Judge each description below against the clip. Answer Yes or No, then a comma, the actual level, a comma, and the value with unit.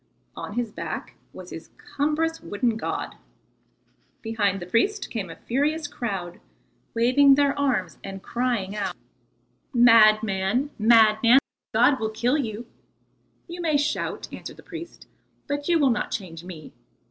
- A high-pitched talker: Yes, high, 235 Hz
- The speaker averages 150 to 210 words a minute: No, average, 140 wpm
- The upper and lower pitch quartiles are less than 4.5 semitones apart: No, wide, 5.6 semitones